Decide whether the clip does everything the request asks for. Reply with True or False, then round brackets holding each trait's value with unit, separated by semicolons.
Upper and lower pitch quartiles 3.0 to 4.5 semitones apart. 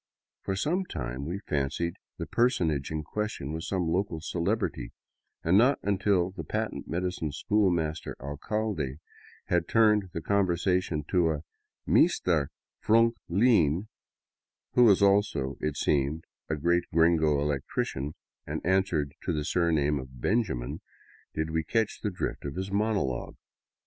False (5.1 semitones)